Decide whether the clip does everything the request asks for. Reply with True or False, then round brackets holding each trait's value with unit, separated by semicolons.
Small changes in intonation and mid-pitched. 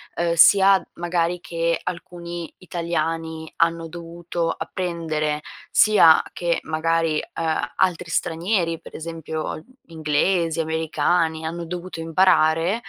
True (1.3 semitones; 165 Hz)